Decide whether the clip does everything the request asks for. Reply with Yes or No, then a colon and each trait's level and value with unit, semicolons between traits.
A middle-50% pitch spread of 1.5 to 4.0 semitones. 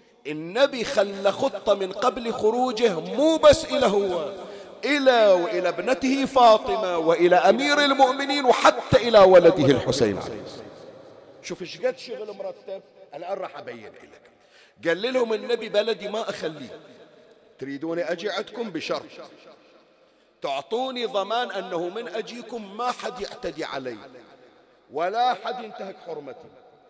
No: average, 5.2 semitones